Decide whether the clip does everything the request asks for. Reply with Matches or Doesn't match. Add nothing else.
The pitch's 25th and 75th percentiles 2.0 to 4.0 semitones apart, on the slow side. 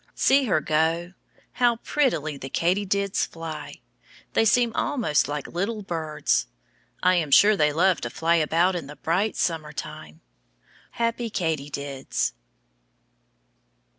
Doesn't match